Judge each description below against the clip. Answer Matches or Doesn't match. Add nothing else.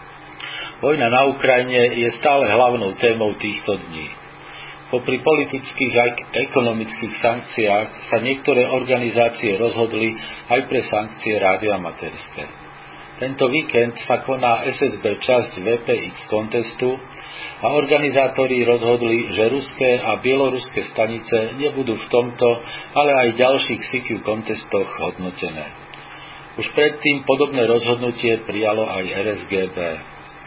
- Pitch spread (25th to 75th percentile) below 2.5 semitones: Doesn't match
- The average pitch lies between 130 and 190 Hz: Doesn't match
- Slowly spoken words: Matches